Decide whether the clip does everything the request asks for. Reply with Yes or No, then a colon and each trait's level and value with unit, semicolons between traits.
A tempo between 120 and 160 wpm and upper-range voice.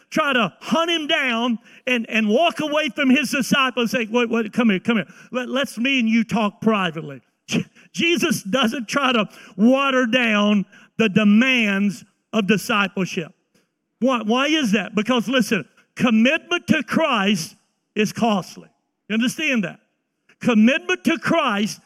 Yes: average, 145 wpm; high, 230 Hz